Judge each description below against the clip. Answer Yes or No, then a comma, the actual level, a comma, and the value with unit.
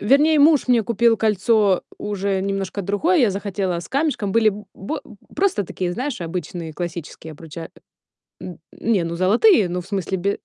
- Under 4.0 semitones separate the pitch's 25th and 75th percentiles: No, average, 4.3 semitones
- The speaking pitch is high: Yes, high, 200 Hz